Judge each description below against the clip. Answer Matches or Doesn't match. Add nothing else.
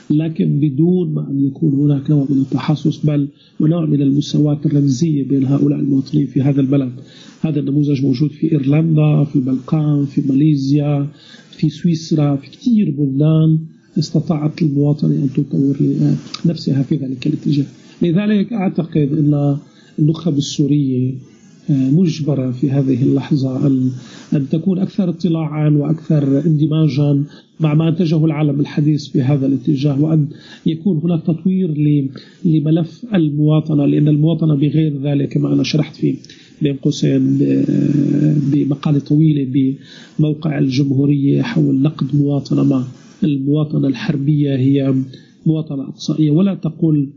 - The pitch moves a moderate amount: Doesn't match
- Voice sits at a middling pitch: Matches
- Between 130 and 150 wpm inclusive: Doesn't match